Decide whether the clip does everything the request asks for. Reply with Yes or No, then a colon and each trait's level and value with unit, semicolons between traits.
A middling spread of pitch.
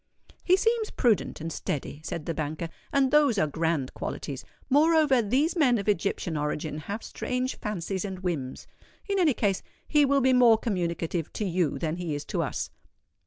No: wide, 8.4 semitones